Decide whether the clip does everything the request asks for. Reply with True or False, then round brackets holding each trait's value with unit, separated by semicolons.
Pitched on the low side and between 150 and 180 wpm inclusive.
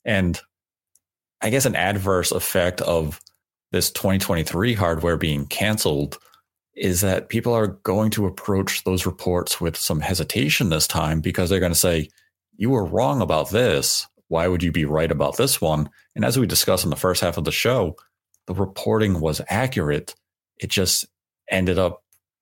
True (90 Hz; 170 wpm)